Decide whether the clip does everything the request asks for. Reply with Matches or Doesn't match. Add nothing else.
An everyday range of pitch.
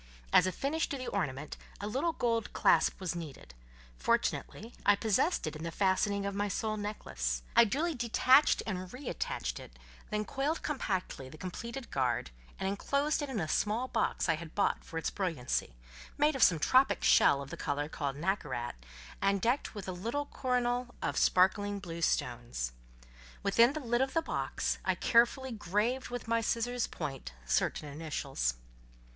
Doesn't match